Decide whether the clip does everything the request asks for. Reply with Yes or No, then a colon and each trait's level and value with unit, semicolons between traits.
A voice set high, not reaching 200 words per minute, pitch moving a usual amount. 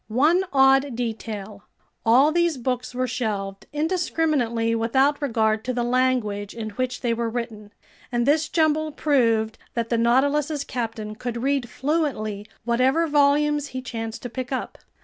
Yes: very high, 250 Hz; average, 150 wpm; average, 4.0 semitones